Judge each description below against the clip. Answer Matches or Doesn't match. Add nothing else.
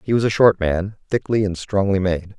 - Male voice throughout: Matches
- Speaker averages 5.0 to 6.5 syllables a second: Matches